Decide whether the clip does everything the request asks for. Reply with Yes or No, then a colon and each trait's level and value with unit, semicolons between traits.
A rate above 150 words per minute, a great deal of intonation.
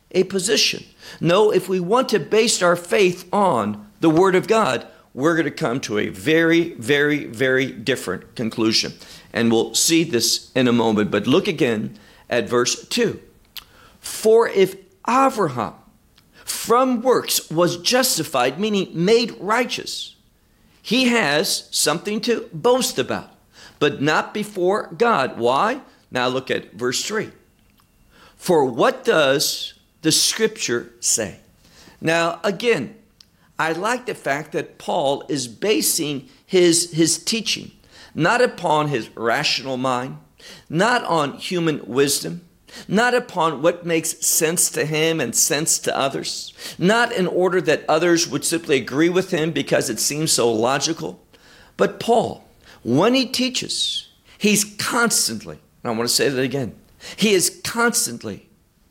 No: average, 140 wpm; wide, 7.2 semitones